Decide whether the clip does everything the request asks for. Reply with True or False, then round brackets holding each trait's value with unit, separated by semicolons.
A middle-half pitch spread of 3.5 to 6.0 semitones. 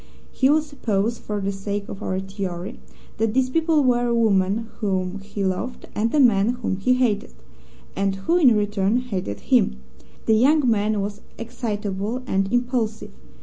True (3.9 semitones)